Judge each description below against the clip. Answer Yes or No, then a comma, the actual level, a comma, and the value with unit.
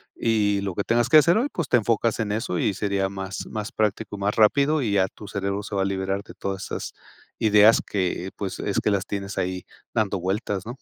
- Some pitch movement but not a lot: No, narrow, 2.1 semitones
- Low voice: Yes, low, 100 Hz